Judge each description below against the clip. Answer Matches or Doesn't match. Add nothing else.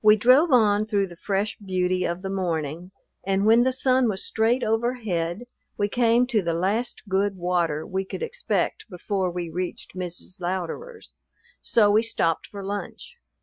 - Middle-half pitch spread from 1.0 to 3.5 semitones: Doesn't match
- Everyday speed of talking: Matches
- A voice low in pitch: Doesn't match